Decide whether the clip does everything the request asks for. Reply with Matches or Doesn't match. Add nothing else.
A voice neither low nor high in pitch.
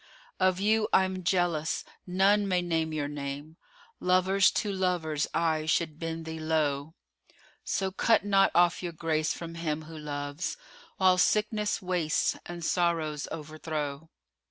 Matches